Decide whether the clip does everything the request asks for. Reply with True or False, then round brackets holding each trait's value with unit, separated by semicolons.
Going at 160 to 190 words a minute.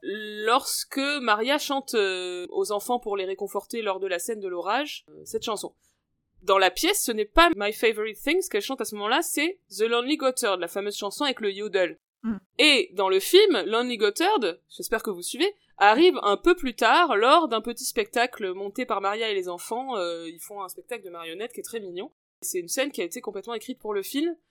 False (210 wpm)